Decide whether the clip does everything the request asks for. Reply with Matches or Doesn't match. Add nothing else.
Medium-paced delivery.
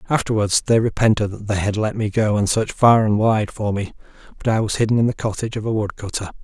Doesn't match